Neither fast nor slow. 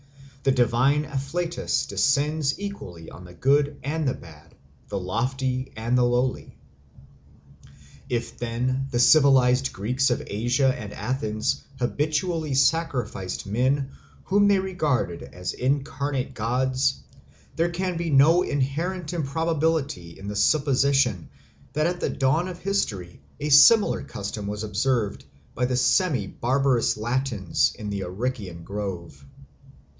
No: slow, 125 wpm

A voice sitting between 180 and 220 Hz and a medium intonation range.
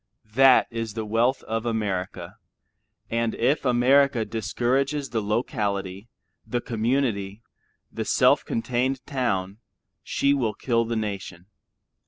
No: low, 115 Hz; average, 3.3 semitones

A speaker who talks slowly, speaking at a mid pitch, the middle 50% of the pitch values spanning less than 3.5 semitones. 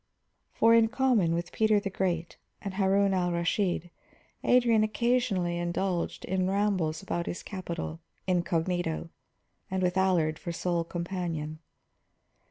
Yes: slow, 125 wpm; medium, 180 Hz; average, 2.8 semitones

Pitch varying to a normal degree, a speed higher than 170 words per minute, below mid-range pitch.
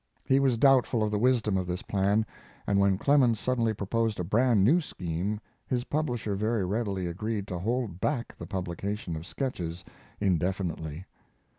No: average, 4.5 semitones; average, 160 wpm; low, 105 Hz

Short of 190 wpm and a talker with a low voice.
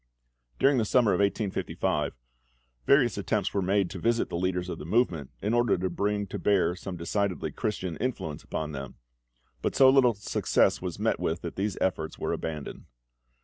Yes: average, 180 wpm; very low, 95 Hz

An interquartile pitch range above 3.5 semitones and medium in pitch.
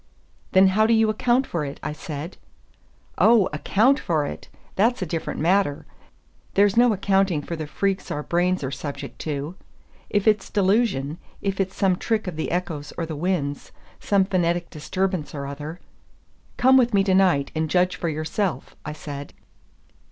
Yes: average, 4.7 semitones; medium, 180 Hz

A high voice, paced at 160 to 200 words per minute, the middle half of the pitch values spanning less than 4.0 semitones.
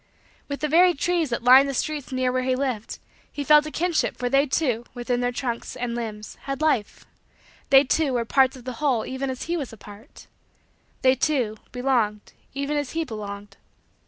Yes: very high, 260 Hz; average, 195 wpm; average, 3.4 semitones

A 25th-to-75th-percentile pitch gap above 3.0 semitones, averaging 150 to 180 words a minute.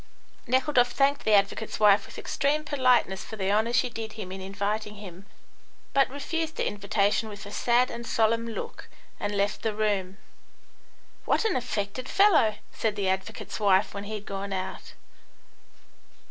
Yes: average, 3.6 semitones; average, 160 wpm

